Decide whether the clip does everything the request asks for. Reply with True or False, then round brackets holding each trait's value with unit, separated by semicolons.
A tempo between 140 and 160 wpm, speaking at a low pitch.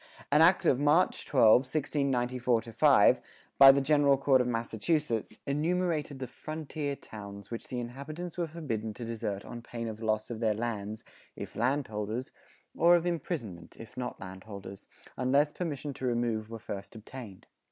True (155 wpm; 125 Hz)